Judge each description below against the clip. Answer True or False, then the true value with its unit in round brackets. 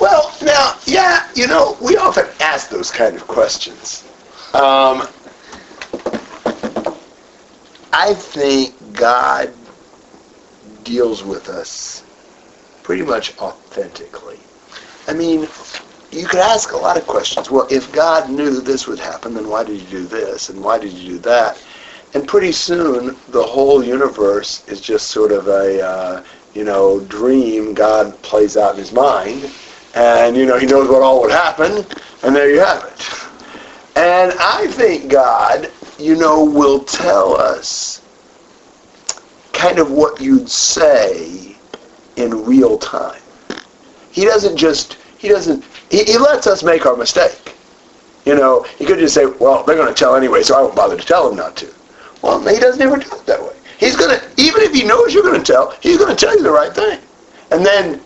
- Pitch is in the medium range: True (155 Hz)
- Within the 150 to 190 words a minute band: True (170 wpm)